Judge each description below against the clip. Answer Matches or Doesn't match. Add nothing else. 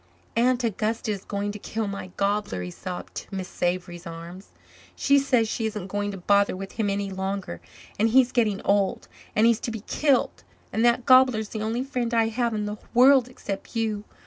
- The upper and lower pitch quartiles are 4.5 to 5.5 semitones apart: Doesn't match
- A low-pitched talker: Doesn't match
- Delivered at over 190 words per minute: Matches